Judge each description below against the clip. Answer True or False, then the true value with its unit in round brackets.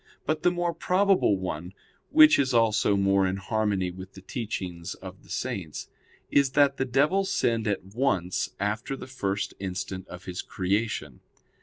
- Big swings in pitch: True (6.3 semitones)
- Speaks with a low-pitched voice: True (100 Hz)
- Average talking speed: True (160 wpm)